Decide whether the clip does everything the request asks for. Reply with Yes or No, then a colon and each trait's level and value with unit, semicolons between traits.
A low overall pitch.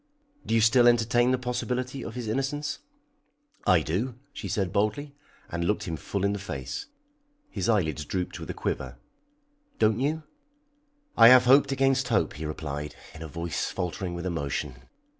Yes: low, 105 Hz